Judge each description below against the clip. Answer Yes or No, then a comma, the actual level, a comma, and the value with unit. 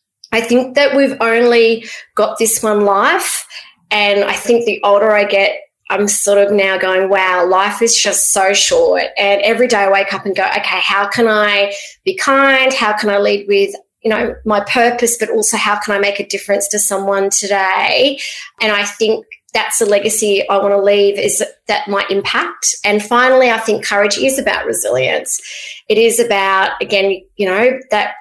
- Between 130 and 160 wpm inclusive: No, average, 195 wpm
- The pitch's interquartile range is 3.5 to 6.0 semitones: No, average, 2.9 semitones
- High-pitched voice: Yes, high, 210 Hz